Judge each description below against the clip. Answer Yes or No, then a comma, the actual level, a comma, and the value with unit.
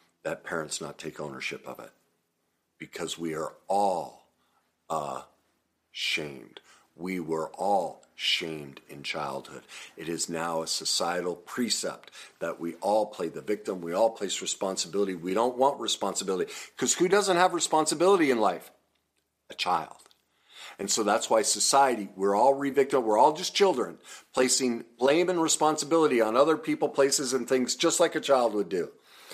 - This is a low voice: Yes, low, 130 Hz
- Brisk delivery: No, average, 155 wpm